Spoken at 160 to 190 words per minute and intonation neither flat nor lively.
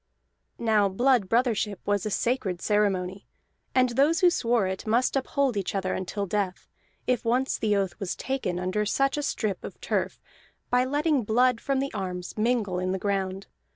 Yes: average, 175 wpm; average, 4.7 semitones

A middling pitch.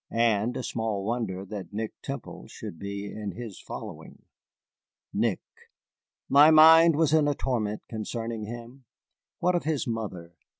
No: low, 115 Hz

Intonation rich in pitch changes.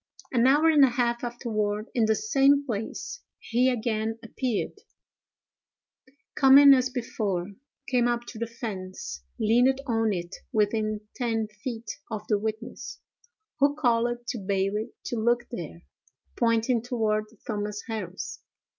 No: narrow, 2.6 semitones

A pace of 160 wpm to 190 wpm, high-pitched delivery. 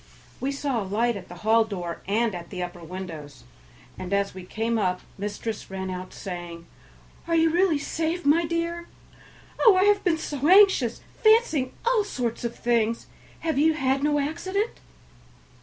Yes: average, 170 wpm; high, 240 Hz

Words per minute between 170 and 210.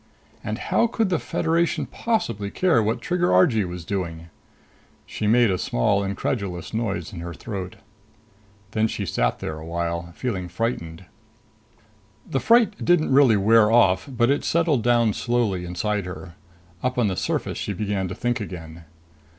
No: average, 160 wpm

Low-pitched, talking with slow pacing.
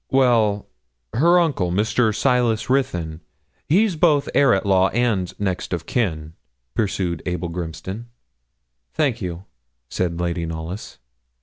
Yes: low, 100 Hz; slow, 120 wpm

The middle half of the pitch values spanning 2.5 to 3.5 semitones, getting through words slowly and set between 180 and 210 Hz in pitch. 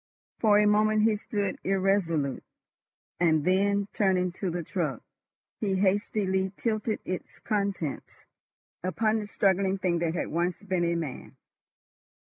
Yes: average, 2.9 semitones; slow, 130 wpm; high, 190 Hz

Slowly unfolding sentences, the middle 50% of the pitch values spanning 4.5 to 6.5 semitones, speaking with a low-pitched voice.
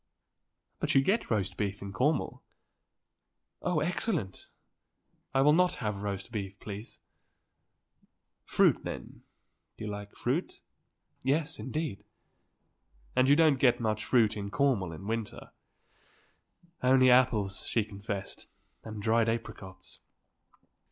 Yes: slow, 115 wpm; average, 5.0 semitones; low, 110 Hz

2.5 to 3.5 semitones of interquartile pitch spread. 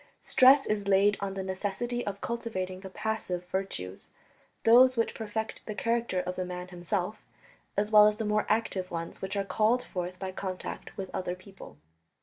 Yes: average, 3.0 semitones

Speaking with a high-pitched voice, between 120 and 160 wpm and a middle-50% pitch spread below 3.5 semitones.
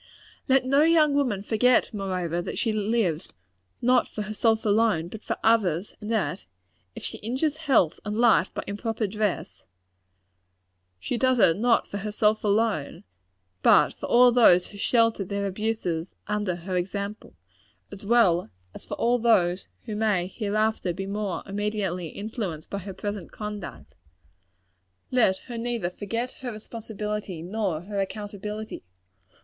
Yes: high, 210 Hz; average, 145 wpm; average, 3.1 semitones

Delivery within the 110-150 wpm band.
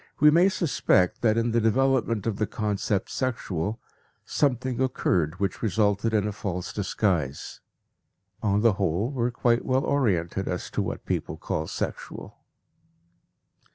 Yes: average, 145 wpm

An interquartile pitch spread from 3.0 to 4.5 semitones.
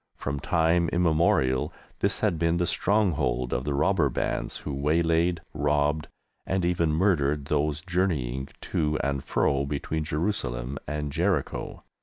Yes: average, 3.4 semitones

